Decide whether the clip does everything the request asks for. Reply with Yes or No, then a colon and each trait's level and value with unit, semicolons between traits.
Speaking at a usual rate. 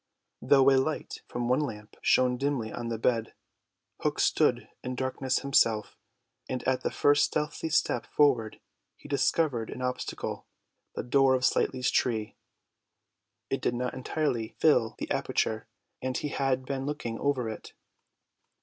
Yes: average, 150 wpm